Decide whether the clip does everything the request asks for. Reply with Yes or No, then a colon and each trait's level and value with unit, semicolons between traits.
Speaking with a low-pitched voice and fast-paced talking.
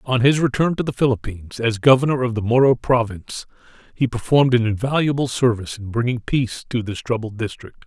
No: low, 120 Hz; average, 185 wpm